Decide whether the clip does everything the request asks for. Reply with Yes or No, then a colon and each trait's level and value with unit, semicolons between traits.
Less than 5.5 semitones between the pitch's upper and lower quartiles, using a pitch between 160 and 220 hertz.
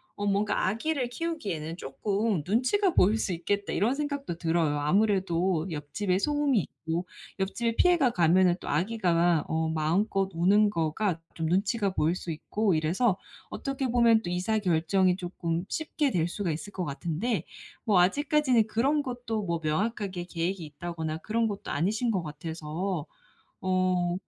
Yes: average, 5.1 semitones; high, 190 Hz